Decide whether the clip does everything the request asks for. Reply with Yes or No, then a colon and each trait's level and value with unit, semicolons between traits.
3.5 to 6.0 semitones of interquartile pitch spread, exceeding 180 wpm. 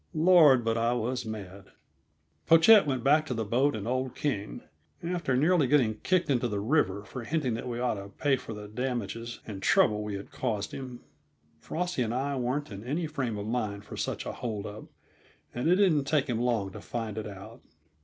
Yes: average, 4.8 semitones; fast, 205 wpm